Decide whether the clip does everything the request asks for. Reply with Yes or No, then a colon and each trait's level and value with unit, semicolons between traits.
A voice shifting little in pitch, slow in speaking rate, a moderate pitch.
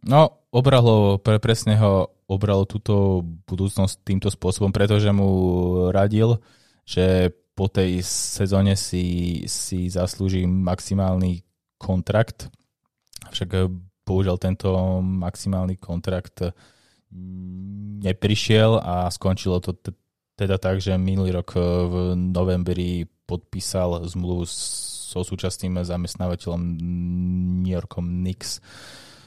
No: narrow, 1.7 semitones; slow, 95 wpm; very low, 95 Hz